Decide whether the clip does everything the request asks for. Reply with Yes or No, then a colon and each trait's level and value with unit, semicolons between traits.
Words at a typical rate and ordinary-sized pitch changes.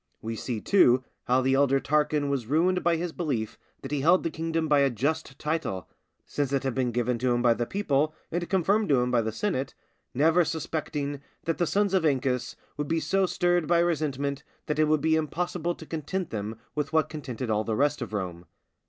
No: fast, 210 wpm; average, 4.5 semitones